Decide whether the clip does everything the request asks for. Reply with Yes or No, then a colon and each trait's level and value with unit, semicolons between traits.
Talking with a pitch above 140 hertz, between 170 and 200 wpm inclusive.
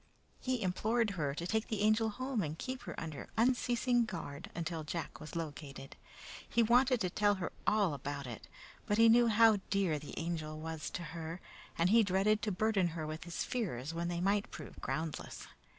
Yes: medium, 185 Hz; average, 190 wpm